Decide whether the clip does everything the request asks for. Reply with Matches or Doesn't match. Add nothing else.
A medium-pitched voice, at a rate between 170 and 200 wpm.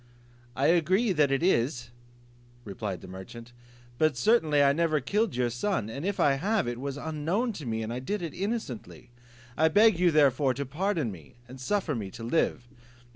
Matches